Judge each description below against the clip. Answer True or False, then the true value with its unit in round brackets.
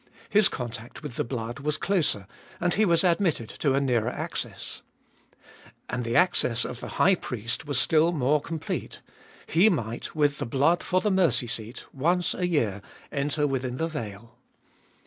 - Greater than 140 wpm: True (165 wpm)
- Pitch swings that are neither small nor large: False (5.8 semitones)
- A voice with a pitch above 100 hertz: True (140 Hz)